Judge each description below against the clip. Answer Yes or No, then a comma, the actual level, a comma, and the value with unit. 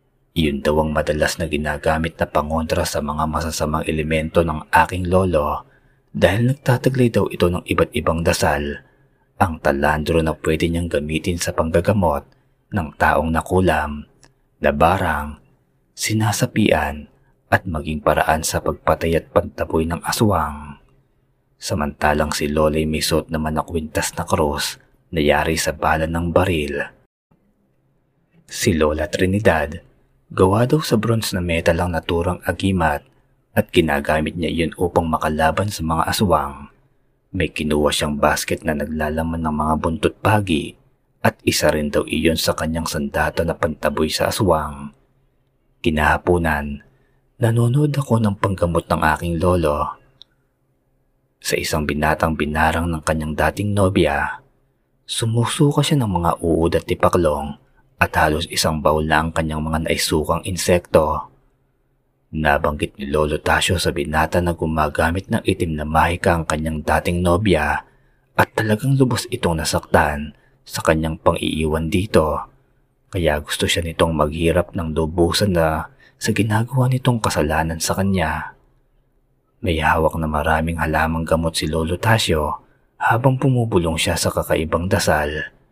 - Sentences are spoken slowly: No, average, 135 wpm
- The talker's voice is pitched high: No, very low, 80 Hz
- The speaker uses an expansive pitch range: No, average, 2.8 semitones